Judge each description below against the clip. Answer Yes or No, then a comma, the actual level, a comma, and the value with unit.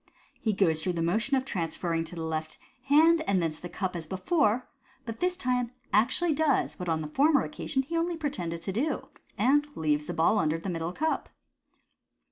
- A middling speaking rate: No, fast, 220 wpm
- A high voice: Yes, high, 200 Hz